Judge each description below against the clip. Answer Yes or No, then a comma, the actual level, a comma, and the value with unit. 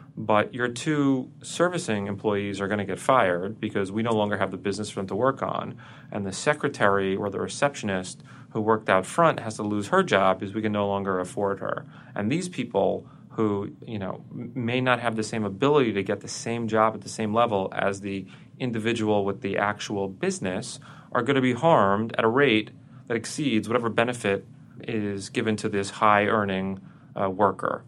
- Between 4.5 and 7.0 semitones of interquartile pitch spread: No, average, 4.0 semitones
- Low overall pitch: Yes, low, 110 Hz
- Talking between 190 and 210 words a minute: Yes, average, 200 wpm